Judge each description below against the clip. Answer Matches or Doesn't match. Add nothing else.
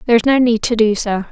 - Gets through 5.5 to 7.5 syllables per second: Matches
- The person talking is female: Matches